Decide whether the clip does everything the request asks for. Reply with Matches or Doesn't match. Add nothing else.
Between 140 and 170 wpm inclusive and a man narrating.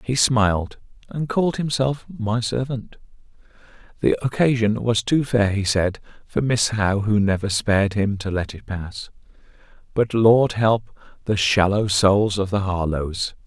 Matches